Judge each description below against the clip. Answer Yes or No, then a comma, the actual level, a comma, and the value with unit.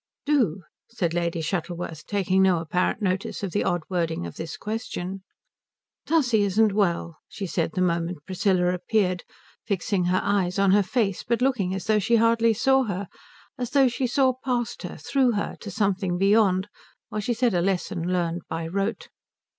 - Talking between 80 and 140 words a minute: No, average, 175 wpm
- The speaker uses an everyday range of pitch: Yes, average, 4.0 semitones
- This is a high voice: Yes, high, 195 Hz